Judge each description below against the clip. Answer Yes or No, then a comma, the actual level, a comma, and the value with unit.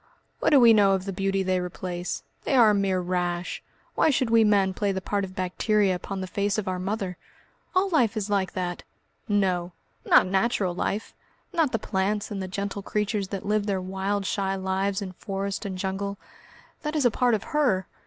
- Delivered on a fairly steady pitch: Yes, narrow, 2.0 semitones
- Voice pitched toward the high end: Yes, high, 195 Hz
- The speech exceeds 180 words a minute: Yes, average, 200 wpm